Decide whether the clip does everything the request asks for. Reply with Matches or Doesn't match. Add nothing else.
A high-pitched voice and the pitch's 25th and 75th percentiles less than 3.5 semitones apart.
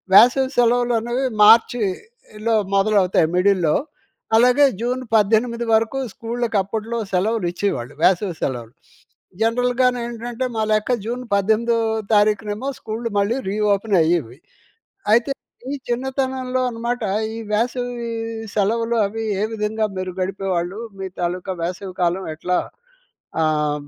Doesn't match